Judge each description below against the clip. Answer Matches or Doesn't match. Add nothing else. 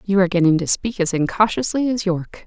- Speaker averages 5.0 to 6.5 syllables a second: Matches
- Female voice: Matches